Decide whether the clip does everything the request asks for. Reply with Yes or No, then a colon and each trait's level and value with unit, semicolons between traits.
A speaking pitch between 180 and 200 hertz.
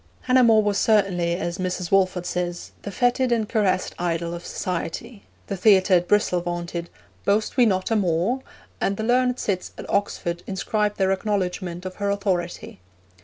Yes: high, 190 Hz